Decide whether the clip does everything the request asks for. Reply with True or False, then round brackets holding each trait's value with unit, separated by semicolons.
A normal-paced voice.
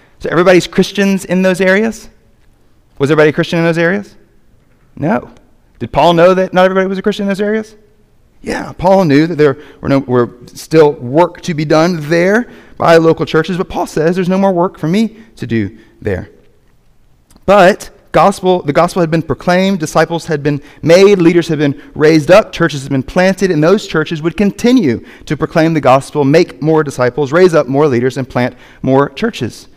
True (190 wpm)